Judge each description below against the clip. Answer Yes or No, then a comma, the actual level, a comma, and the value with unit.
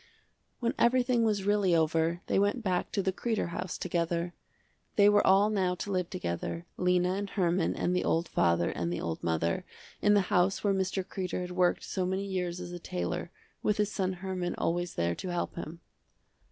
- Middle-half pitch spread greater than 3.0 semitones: No, average, 2.7 semitones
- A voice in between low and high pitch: Yes, medium, 180 Hz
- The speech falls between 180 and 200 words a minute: Yes, average, 195 wpm